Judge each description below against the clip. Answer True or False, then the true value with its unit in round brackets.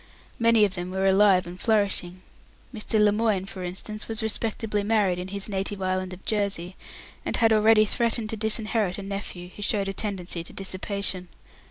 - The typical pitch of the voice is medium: False (200 Hz)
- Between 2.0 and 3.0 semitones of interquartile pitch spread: True (2.5 semitones)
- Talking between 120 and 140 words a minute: False (175 wpm)